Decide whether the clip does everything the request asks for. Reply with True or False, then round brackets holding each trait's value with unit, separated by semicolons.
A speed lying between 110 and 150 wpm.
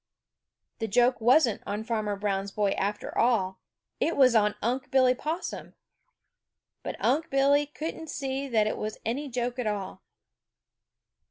True (145 wpm)